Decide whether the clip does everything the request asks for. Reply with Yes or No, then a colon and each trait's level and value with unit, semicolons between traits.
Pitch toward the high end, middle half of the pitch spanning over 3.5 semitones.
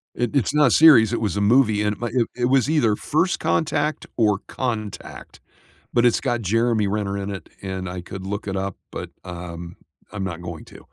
No: low, 105 Hz; average, 4.1 semitones